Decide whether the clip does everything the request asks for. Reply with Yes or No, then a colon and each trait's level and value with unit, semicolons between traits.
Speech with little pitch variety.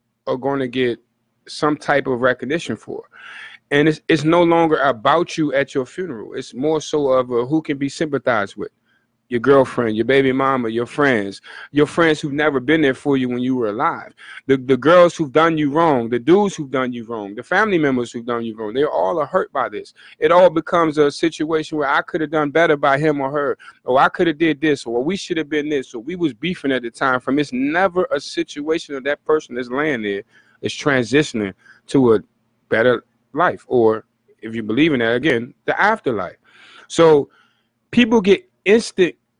No: average, 4.6 semitones